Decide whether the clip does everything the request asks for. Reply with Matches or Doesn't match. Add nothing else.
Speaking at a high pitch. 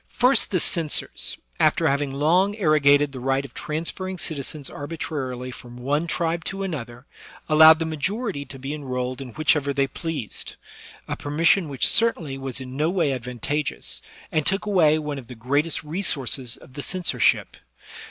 Doesn't match